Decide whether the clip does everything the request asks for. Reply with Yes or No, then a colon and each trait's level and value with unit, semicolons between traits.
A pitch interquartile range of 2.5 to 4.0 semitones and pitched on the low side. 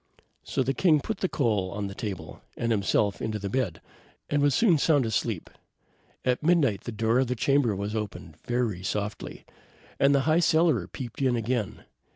No: average, 5.1 semitones; low, 120 Hz